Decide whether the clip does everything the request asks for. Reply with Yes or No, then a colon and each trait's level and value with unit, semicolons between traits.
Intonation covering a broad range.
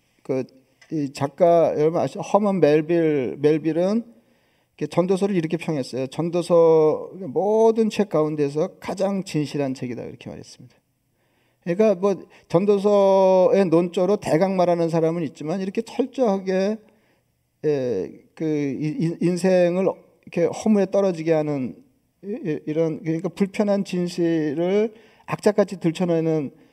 No: average, 4.3 semitones